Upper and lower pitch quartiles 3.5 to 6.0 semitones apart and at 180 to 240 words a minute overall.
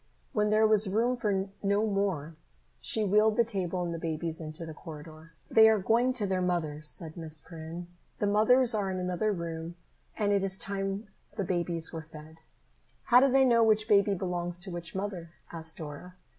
Yes: average, 4.2 semitones; average, 190 wpm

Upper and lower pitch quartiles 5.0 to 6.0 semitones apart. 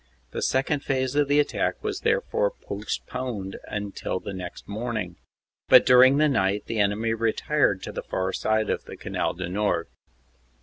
Yes: wide, 5.5 semitones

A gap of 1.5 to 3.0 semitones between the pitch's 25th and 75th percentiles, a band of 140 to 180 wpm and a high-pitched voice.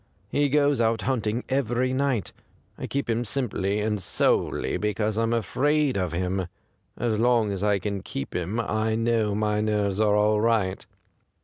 No: average, 2.7 semitones; average, 165 wpm; low, 110 Hz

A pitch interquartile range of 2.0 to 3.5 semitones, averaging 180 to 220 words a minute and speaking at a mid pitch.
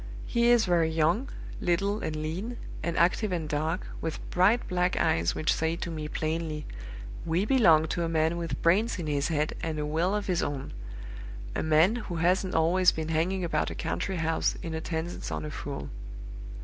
Yes: average, 2.7 semitones; average, 190 wpm; medium, 165 Hz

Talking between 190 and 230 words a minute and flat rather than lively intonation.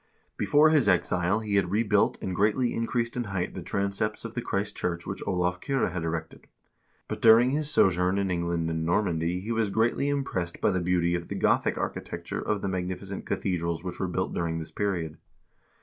No: average, 195 wpm; average, 3.9 semitones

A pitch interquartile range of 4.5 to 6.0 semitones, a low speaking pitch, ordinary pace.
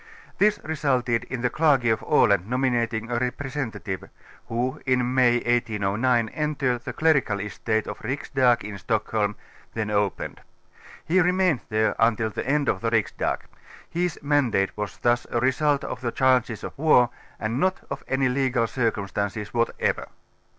No: average, 3.6 semitones; low, 120 Hz; average, 150 wpm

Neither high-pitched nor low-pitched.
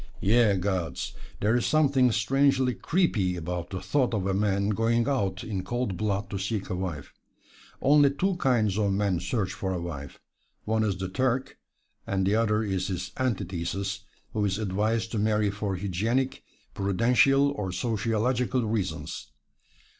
No: low, 105 Hz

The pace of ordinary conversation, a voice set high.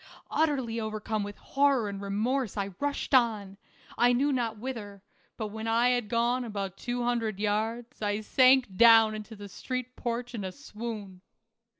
Yes: average, 165 wpm; high, 225 Hz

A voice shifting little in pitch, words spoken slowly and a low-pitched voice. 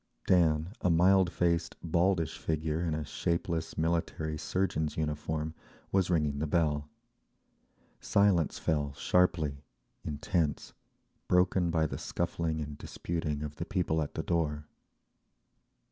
Yes: narrow, 2.2 semitones; slow, 120 wpm; very low, 80 Hz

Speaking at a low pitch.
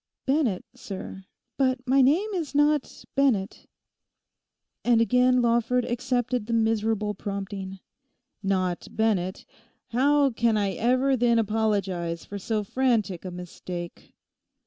No: high, 225 Hz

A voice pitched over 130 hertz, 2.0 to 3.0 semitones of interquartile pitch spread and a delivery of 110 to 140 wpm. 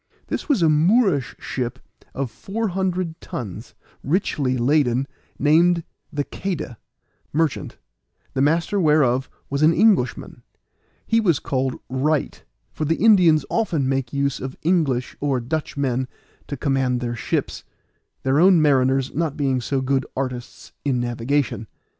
No: medium, 140 Hz; average, 4.2 semitones; slow, 135 wpm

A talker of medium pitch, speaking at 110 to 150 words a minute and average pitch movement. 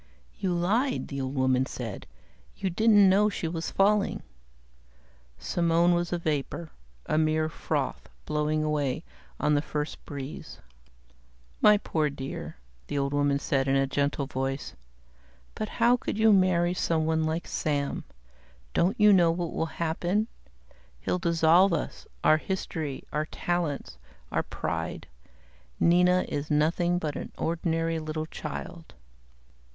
Yes: medium, 160 Hz; slow, 135 wpm; average, 3.3 semitones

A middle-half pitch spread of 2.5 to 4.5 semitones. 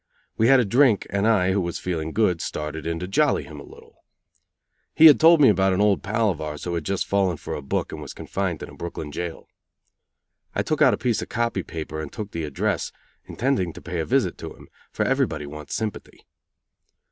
No: average, 5.3 semitones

